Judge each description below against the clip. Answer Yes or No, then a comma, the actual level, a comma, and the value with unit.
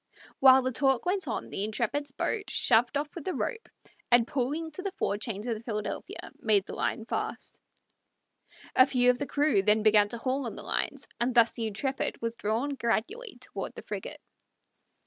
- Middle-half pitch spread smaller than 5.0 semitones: Yes, average, 4.3 semitones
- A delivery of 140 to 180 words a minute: No, average, 190 wpm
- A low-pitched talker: No, high, 245 Hz